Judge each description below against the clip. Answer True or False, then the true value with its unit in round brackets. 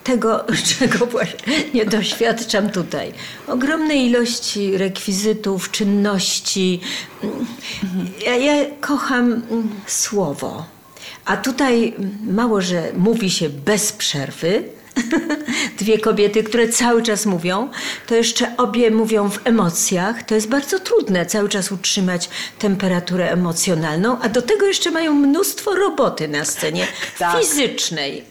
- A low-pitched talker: False (220 Hz)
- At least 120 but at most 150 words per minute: False (110 wpm)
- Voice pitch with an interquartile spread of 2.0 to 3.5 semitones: False (4.3 semitones)